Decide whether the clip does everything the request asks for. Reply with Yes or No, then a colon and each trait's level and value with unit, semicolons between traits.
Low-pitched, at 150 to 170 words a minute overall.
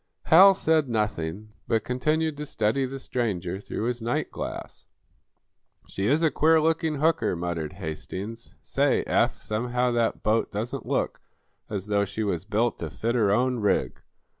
Yes: low, 115 Hz; average, 160 wpm